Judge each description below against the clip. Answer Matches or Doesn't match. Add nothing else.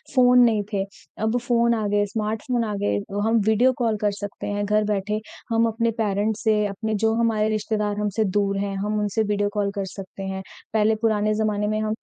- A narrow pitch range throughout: Matches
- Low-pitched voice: Doesn't match